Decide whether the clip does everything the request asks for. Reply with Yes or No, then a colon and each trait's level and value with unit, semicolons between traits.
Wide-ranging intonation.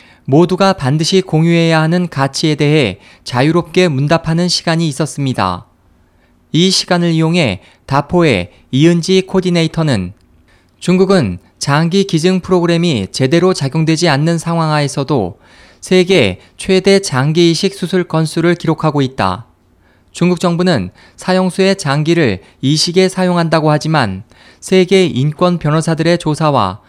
Yes: wide, 6.1 semitones